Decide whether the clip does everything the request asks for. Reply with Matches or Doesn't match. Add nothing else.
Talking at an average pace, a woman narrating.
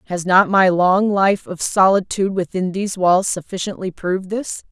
Matches